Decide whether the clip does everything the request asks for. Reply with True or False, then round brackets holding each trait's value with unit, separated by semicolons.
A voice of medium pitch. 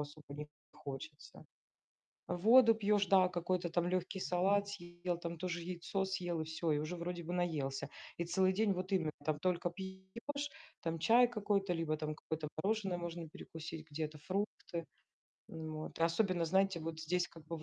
True (175 Hz)